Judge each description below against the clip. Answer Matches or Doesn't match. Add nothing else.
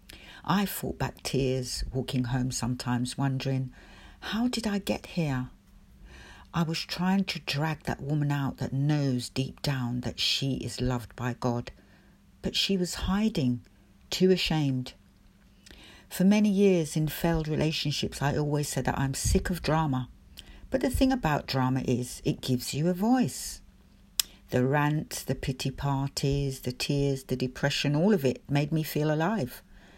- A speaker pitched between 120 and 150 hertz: Matches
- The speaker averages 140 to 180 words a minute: Matches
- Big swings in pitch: Doesn't match